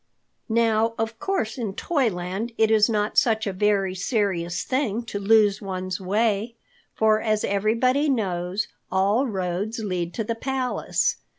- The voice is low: No, high, 215 Hz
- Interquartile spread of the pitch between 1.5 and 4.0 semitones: Yes, average, 2.9 semitones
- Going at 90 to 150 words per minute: Yes, average, 140 wpm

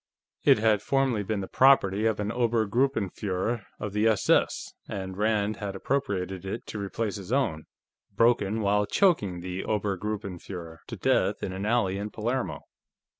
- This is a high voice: No, low, 105 Hz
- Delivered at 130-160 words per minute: Yes, average, 150 wpm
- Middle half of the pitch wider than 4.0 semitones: No, average, 2.8 semitones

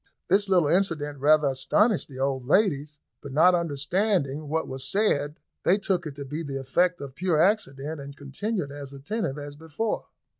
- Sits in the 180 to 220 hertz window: No, medium, 150 Hz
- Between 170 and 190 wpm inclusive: Yes, average, 175 wpm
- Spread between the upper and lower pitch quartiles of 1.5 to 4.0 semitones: No, average, 4.6 semitones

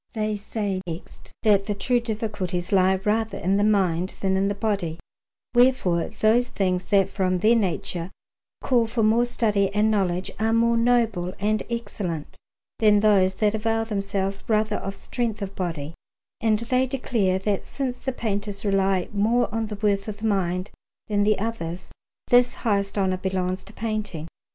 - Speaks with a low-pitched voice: No, high, 205 Hz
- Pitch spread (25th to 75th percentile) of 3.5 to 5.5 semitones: No, average, 2.8 semitones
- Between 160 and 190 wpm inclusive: Yes, average, 165 wpm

